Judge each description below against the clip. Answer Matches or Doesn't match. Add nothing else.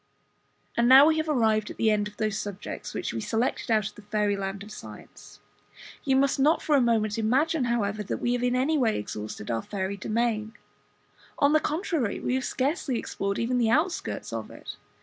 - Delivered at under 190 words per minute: Doesn't match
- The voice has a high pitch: Matches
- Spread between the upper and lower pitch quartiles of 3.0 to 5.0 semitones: Matches